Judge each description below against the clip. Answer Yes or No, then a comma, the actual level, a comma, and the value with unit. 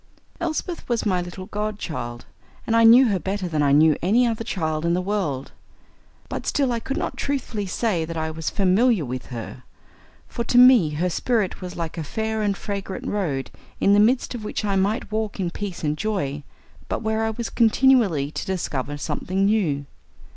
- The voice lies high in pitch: Yes, high, 195 Hz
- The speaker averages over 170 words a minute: Yes, average, 190 wpm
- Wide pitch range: Yes, wide, 5.7 semitones